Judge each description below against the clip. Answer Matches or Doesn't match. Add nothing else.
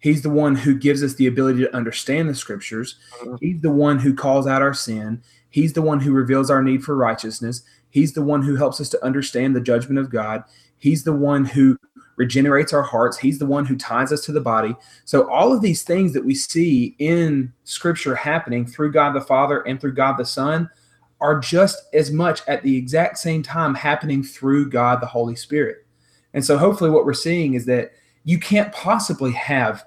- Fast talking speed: Matches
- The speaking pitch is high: Doesn't match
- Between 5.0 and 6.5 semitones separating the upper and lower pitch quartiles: Doesn't match